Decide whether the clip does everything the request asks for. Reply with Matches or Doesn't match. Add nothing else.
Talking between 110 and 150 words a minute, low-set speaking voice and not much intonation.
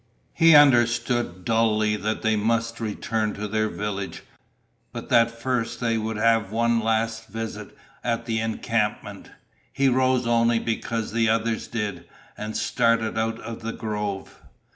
Matches